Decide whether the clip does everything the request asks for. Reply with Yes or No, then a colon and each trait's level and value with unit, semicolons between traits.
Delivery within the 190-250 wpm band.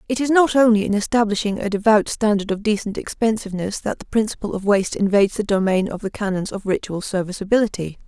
Yes: average, 195 wpm